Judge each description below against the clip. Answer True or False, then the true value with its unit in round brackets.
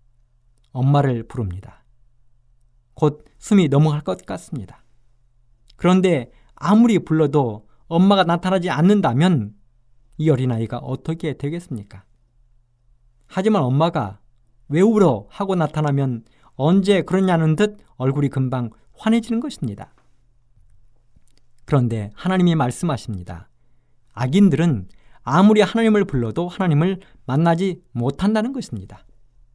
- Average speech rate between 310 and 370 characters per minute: False (260 characters per minute)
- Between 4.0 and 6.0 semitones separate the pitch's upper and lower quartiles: False (6.5 semitones)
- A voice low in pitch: True (130 Hz)